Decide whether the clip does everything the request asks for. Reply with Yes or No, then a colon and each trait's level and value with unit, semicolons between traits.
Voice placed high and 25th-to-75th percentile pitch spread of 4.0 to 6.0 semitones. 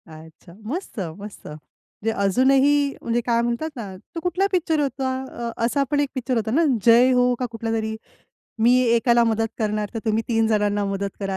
No: high, 235 Hz; average, 3.4 semitones